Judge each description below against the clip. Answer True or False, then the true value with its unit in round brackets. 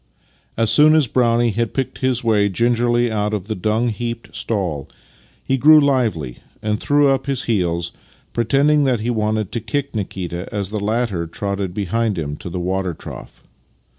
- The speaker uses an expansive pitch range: False (3.8 semitones)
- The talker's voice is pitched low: True (110 Hz)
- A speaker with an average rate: True (170 wpm)